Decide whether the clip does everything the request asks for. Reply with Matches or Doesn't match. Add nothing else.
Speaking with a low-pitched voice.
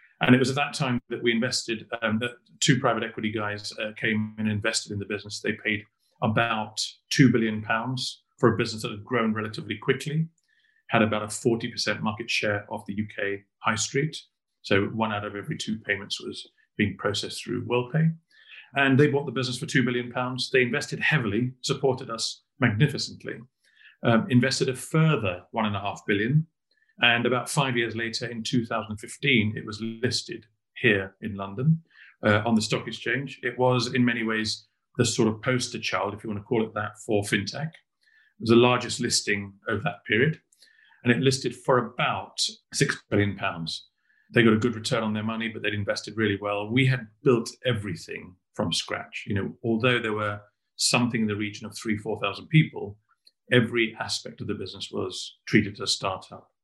Matches